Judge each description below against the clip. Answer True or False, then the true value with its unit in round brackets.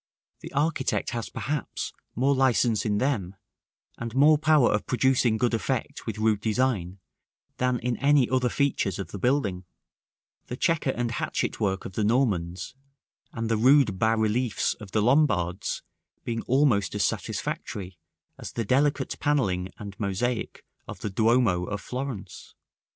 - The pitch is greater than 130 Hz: False (115 Hz)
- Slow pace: False (150 wpm)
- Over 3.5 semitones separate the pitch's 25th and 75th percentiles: True (4.5 semitones)